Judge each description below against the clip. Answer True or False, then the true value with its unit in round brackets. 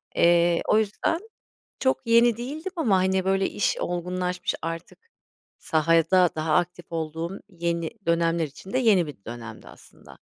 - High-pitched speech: False (175 Hz)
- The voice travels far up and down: False (3.6 semitones)